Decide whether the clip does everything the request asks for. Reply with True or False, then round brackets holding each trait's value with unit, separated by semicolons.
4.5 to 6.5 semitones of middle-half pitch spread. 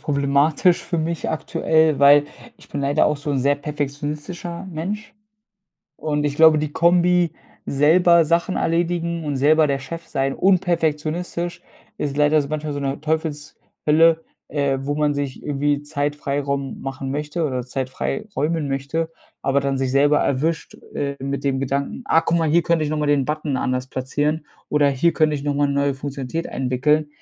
False (2.5 semitones)